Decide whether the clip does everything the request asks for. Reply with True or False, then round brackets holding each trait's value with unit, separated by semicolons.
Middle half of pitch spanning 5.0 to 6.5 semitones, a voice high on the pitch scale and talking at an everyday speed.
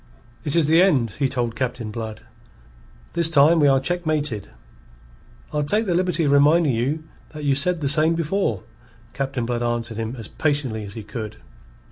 False (5.3 semitones; 140 Hz; 175 wpm)